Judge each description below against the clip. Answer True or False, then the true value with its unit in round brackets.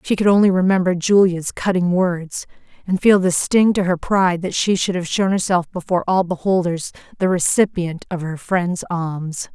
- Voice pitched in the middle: True (180 Hz)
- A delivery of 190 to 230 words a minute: False (180 wpm)